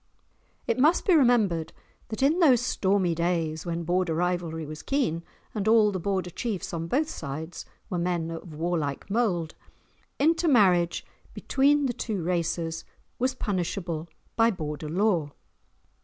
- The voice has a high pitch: No, medium, 180 Hz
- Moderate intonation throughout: No, wide, 5.7 semitones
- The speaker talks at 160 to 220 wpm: No, average, 140 wpm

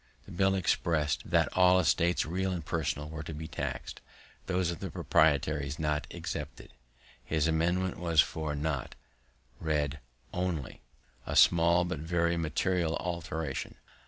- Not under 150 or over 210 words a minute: No, slow, 135 wpm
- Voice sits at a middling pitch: No, very low, 80 Hz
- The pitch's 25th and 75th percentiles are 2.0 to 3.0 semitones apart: Yes, narrow, 2.5 semitones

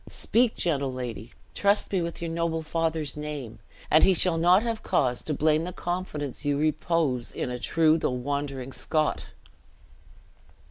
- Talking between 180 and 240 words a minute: No, average, 155 wpm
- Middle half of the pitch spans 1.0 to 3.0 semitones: No, average, 3.6 semitones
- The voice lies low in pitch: No, medium, 155 Hz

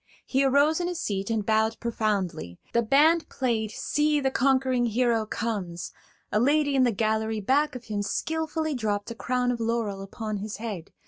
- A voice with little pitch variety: No, average, 4.2 semitones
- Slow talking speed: No, average, 180 wpm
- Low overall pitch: No, high, 235 Hz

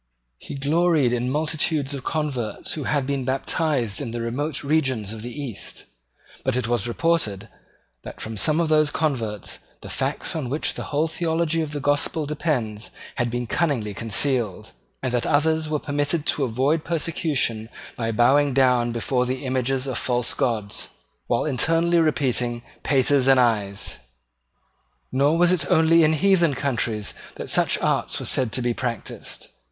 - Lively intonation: No, average, 4.3 semitones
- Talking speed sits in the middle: Yes, average, 160 wpm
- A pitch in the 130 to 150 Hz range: Yes, low, 135 Hz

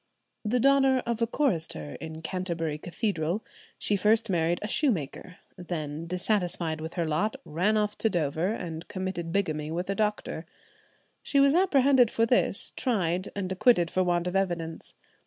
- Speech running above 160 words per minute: No, average, 155 wpm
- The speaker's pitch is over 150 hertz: Yes, medium, 185 Hz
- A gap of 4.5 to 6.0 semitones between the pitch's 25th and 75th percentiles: Yes, average, 4.8 semitones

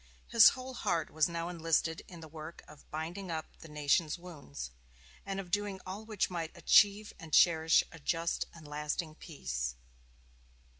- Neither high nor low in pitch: Yes, medium, 165 Hz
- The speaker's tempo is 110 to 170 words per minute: Yes, average, 160 wpm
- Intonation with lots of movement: No, average, 3.2 semitones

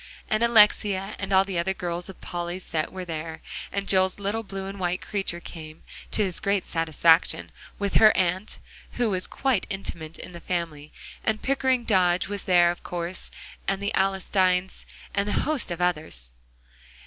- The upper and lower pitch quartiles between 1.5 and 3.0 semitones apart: Yes, narrow, 2.6 semitones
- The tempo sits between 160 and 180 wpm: Yes, average, 170 wpm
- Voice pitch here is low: No, medium, 185 Hz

